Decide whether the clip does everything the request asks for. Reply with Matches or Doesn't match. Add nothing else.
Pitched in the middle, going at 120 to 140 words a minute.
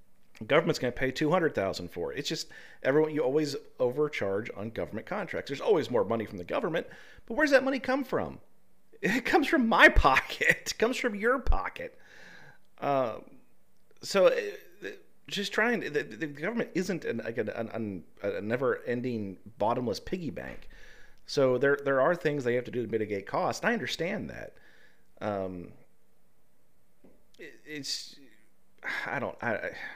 Doesn't match